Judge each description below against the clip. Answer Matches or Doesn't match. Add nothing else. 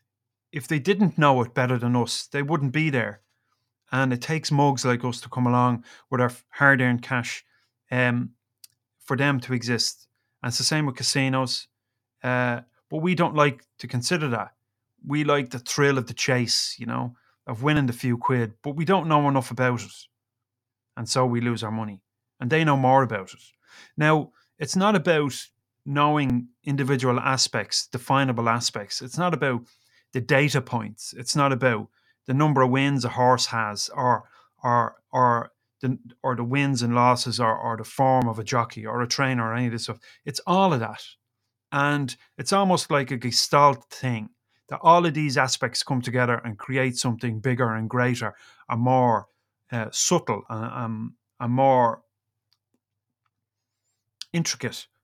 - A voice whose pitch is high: Doesn't match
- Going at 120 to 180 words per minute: Matches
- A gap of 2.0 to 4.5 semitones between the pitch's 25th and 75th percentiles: Matches